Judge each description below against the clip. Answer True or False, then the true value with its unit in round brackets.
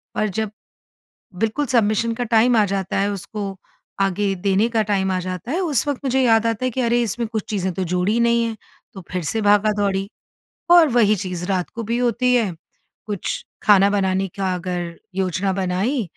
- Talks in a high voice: True (210 Hz)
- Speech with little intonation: False (3.4 semitones)